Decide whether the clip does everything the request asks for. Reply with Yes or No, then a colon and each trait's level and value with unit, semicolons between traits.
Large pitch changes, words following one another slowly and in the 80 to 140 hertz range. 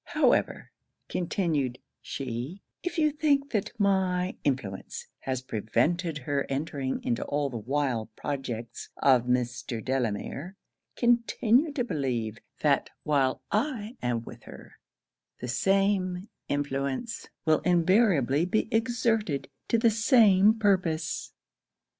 No: wide, 8.1 semitones; slow, 110 wpm; medium, 155 Hz